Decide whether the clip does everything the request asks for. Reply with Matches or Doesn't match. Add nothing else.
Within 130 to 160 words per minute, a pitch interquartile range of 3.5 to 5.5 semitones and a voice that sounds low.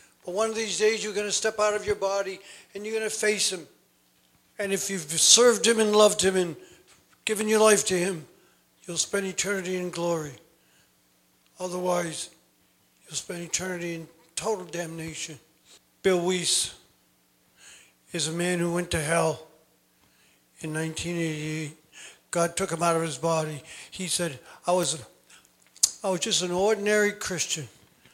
Doesn't match